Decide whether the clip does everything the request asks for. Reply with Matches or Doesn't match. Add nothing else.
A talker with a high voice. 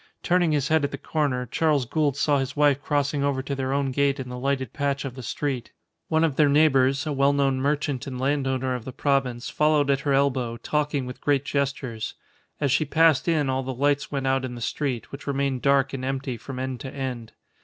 Doesn't match